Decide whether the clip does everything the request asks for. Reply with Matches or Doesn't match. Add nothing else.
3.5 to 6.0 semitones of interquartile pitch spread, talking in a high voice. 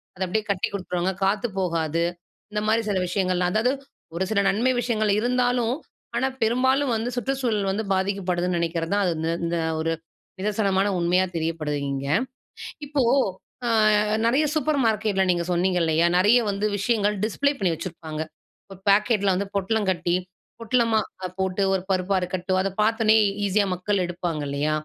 Matches